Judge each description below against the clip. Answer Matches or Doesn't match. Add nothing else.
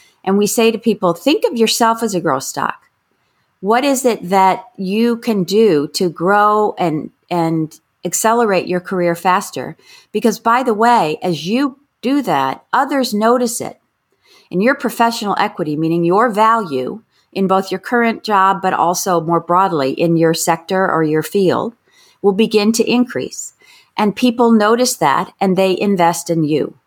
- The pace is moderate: Matches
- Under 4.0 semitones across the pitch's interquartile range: Doesn't match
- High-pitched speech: Matches